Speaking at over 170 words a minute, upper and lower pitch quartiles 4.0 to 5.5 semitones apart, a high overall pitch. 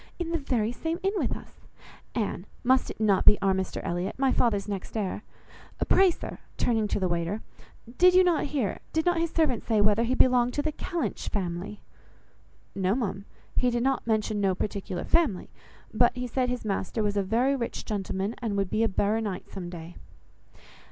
Yes: average, 190 wpm; average, 4.8 semitones; high, 220 Hz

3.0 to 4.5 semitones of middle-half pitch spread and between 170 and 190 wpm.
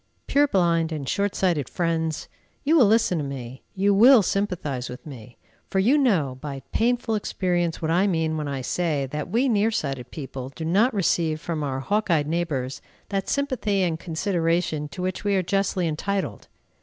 No: average, 5.1 semitones; average, 180 wpm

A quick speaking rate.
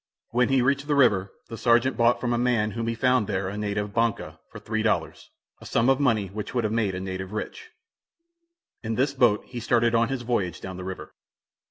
Yes: fast, 215 wpm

